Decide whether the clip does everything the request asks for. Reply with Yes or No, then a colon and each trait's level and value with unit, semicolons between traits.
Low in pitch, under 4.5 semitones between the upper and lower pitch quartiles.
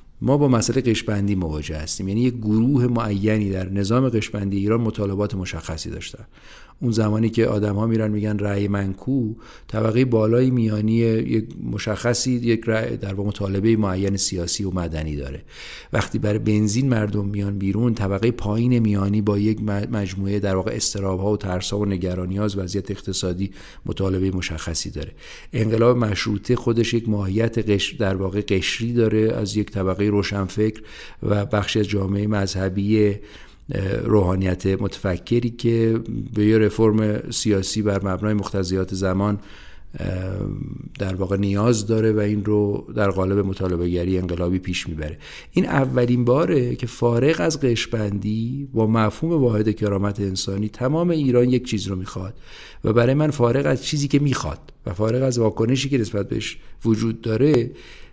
Yes: low, 105 Hz; average, 2.8 semitones